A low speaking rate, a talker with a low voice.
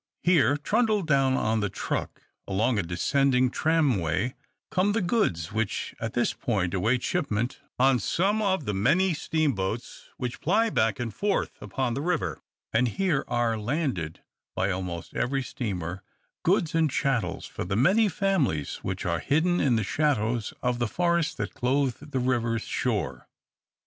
No: average, 160 wpm; low, 125 Hz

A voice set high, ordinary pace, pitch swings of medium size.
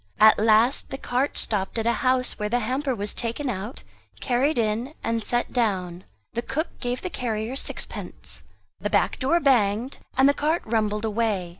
Yes: high, 235 Hz; average, 175 wpm; average, 3.5 semitones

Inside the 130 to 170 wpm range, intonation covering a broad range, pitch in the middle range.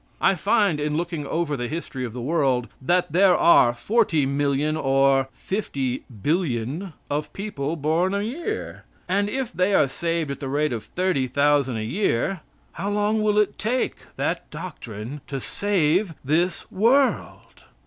Yes: average, 150 wpm; wide, 6.1 semitones; medium, 155 Hz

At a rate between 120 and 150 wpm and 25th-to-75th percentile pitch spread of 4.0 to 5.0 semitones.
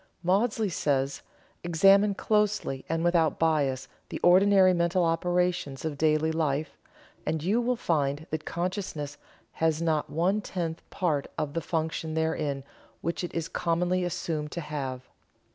No: average, 140 wpm; average, 2.9 semitones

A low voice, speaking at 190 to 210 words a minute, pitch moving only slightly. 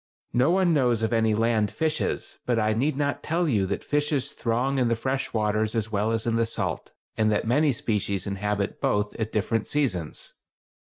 No: low, 115 Hz; average, 195 wpm; average, 4.1 semitones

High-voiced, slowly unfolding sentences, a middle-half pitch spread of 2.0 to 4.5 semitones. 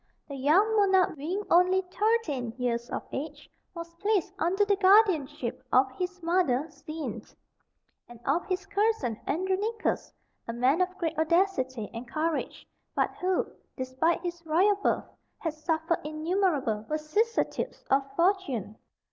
No: very high, 335 Hz; slow, 130 wpm; wide, 5.5 semitones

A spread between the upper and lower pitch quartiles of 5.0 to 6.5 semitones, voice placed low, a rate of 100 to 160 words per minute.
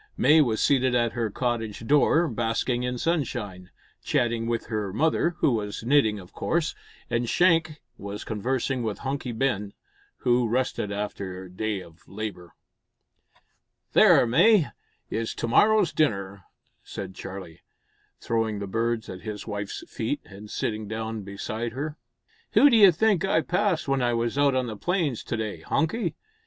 Yes: average, 5.3 semitones; low, 115 Hz; average, 155 wpm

